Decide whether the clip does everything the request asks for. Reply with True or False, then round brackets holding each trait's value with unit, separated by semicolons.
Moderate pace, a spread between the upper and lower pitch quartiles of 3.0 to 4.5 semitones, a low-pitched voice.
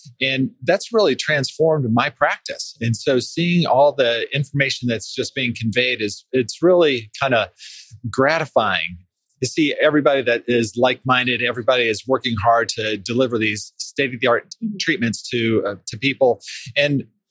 True (150 wpm; 3.5 semitones; 125 Hz)